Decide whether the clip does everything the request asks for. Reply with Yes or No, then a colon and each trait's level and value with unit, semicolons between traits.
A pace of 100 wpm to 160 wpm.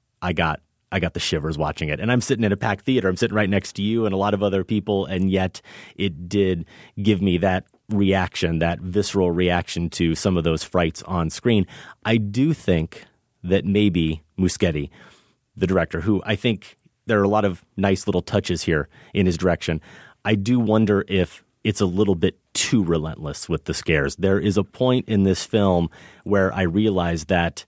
No: average, 200 wpm